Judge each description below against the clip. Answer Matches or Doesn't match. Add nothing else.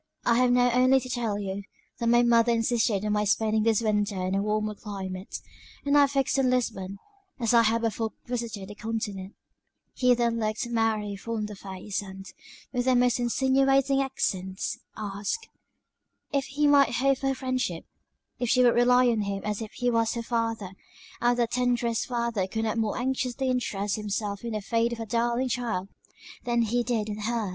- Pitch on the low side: Doesn't match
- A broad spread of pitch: Doesn't match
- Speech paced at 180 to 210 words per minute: Matches